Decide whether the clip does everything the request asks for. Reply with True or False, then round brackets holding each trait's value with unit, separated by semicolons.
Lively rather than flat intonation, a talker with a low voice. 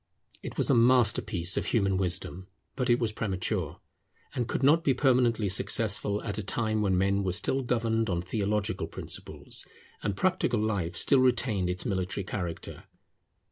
False (4.1 semitones; 105 Hz)